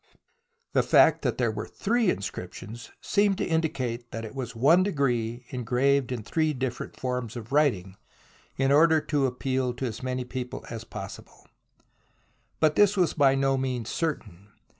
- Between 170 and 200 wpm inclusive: No, average, 160 wpm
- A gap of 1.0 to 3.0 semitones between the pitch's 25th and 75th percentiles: No, average, 4.0 semitones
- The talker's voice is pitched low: Yes, low, 130 Hz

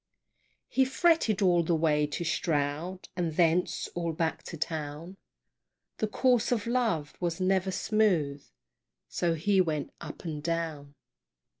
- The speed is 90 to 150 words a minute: Yes, slow, 135 wpm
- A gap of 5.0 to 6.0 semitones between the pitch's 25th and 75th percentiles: No, average, 3.8 semitones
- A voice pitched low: No, medium, 170 Hz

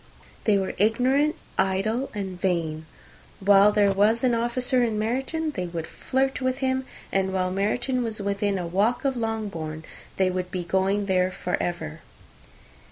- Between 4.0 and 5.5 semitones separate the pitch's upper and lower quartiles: Yes, average, 4.7 semitones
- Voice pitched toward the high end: Yes, high, 205 Hz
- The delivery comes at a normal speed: Yes, average, 160 wpm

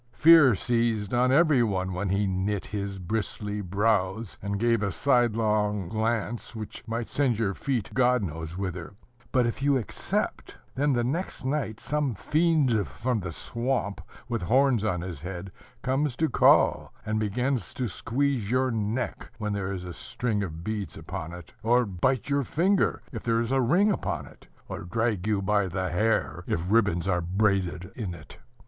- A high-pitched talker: No, low, 110 Hz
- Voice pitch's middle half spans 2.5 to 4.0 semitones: No, average, 4.6 semitones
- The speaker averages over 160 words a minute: Yes, average, 175 wpm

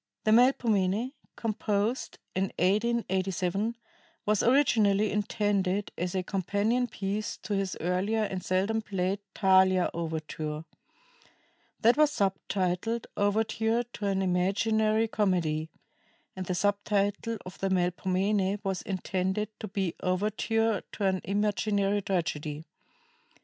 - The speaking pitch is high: Yes, high, 200 Hz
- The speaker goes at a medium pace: No, slow, 115 wpm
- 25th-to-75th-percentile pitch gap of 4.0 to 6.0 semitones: No, narrow, 2.6 semitones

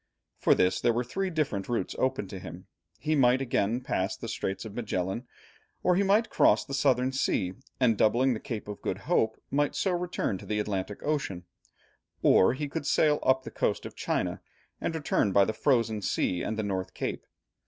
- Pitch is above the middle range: No, low, 120 Hz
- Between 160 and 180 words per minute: No, average, 195 wpm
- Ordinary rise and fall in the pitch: No, wide, 5.7 semitones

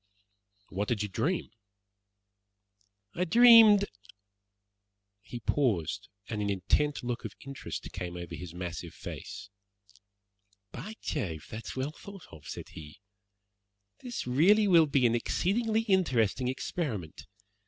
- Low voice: Yes, low, 125 Hz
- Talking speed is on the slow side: Yes, slow, 120 wpm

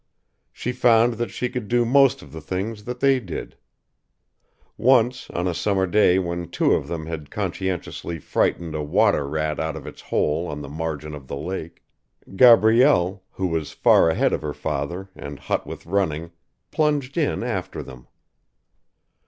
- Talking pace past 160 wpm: Yes, average, 170 wpm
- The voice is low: Yes, very low, 90 Hz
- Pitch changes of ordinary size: No, wide, 6.8 semitones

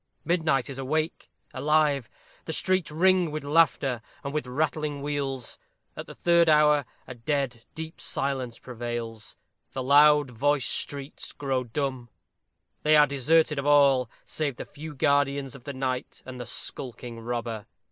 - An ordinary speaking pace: Yes, average, 145 wpm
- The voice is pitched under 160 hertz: Yes, medium, 140 Hz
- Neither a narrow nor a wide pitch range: Yes, average, 3.0 semitones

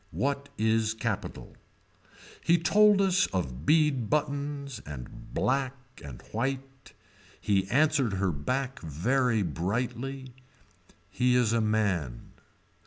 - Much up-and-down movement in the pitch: Yes, wide, 5.9 semitones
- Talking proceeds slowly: Yes, slow, 105 wpm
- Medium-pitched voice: No, low, 125 Hz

